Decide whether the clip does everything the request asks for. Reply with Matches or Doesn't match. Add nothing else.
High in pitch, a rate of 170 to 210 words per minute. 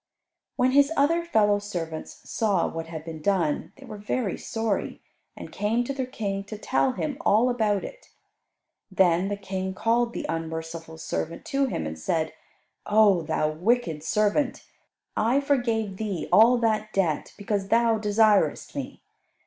Doesn't match